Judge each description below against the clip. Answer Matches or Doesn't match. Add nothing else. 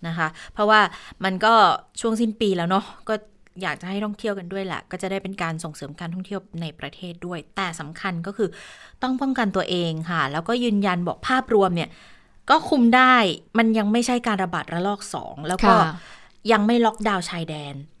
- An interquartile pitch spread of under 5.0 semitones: Matches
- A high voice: Matches